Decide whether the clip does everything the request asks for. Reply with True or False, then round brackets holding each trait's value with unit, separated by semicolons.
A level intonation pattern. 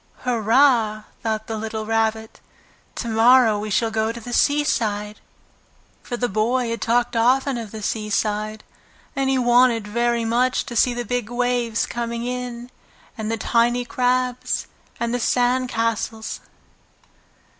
True (2.0 semitones)